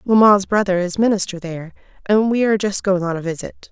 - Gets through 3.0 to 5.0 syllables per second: No, 6.0 syllables/s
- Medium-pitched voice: No, high, 195 Hz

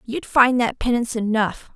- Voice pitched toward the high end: Yes, high, 235 Hz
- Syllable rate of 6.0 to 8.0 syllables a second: No, 4.9 syllables/s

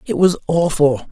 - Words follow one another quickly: No, average, 160 wpm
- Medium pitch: Yes, medium, 155 Hz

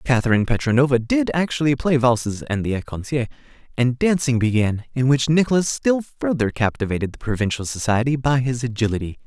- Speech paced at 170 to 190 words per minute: No, average, 155 wpm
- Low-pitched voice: Yes, low, 125 Hz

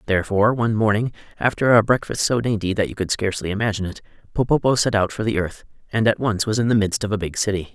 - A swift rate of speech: Yes, fast, 240 wpm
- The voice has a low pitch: Yes, low, 105 Hz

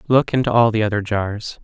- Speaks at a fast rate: Yes, fast, 220 wpm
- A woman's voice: No, male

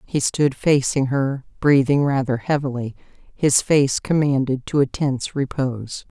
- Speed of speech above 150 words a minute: No, slow, 135 wpm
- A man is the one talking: No, female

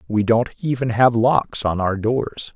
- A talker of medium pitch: No, low, 115 Hz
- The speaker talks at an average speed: Yes, average, 190 wpm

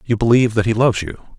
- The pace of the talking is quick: Yes, fast, 260 wpm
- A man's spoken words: Yes, male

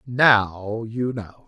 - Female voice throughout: No, male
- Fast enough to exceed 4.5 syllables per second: No, 2.2 syllables/s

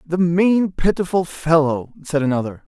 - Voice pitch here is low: No, medium, 165 Hz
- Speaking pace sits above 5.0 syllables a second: No, 4.5 syllables/s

